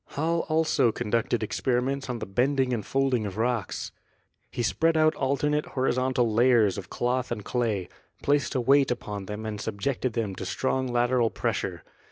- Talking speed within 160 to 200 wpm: Yes, average, 165 wpm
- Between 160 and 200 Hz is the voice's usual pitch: No, low, 125 Hz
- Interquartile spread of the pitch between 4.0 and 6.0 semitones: No, average, 3.5 semitones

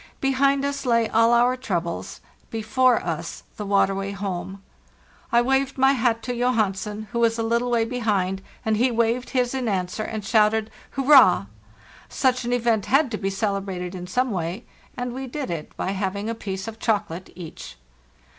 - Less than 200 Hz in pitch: No, high, 225 Hz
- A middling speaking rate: Yes, average, 175 wpm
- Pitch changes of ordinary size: Yes, average, 4.1 semitones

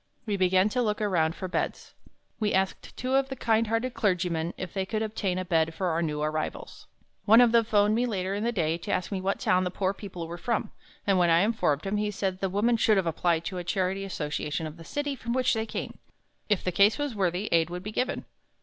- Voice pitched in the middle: No, high, 195 Hz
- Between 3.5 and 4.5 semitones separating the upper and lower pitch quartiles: Yes, average, 4.0 semitones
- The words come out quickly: Yes, fast, 245 wpm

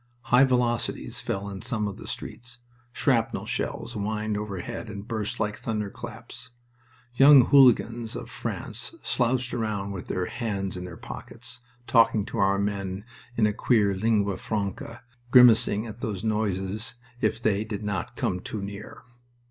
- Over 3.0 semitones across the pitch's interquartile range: No, average, 2.7 semitones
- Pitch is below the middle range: Yes, low, 110 Hz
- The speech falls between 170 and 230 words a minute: No, average, 150 wpm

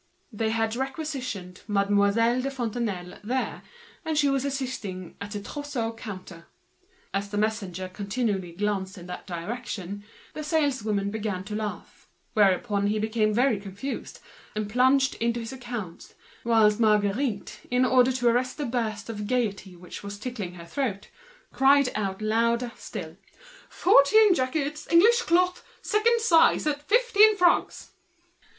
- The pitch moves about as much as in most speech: Yes, average, 4.9 semitones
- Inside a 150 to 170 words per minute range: No, average, 140 wpm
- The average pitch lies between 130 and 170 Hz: No, high, 225 Hz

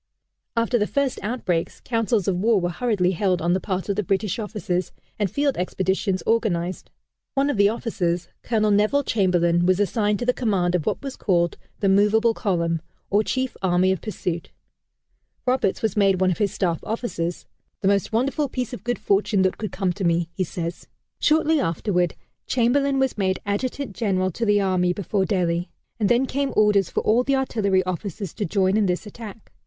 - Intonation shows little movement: No, average, 4.0 semitones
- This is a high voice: Yes, high, 200 Hz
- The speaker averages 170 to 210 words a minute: Yes, average, 190 wpm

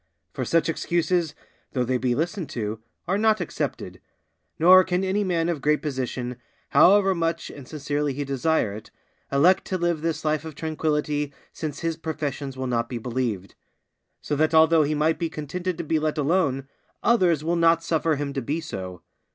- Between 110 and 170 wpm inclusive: No, average, 180 wpm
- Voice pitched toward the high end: No, medium, 155 Hz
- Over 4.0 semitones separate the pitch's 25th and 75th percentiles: No, average, 3.4 semitones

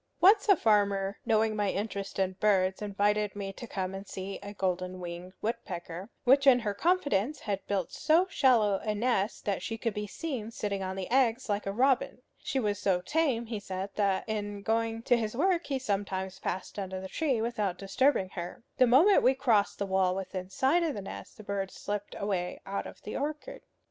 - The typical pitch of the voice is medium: No, high, 205 Hz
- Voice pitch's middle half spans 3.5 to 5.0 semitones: Yes, average, 4.1 semitones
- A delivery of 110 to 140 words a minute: No, average, 200 wpm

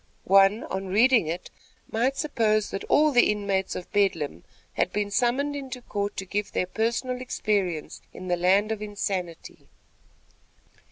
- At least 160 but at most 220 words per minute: No, average, 150 wpm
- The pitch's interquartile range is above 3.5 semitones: Yes, average, 4.0 semitones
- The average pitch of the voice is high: Yes, high, 205 Hz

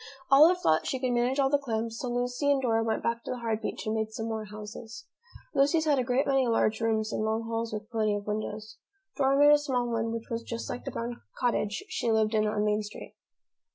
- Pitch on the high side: Yes, high, 230 Hz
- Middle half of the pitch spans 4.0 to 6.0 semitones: No, average, 2.8 semitones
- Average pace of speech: No, fast, 240 wpm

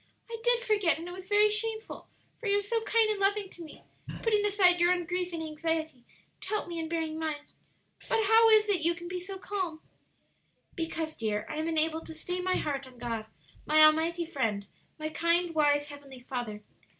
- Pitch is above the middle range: Yes, very high, 335 Hz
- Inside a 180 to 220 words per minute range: Yes, fast, 205 wpm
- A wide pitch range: No, average, 4.5 semitones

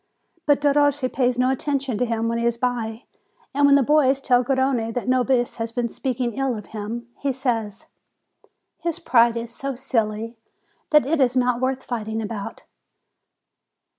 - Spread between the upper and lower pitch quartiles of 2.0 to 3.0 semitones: Yes, average, 2.7 semitones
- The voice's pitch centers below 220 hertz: No, very high, 250 Hz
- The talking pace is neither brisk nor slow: Yes, average, 165 wpm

